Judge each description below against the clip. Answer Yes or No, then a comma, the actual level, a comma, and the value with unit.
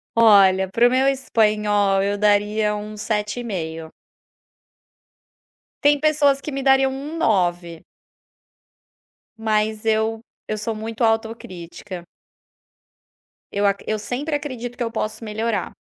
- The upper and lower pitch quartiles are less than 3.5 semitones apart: Yes, average, 3.1 semitones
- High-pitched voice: Yes, high, 220 Hz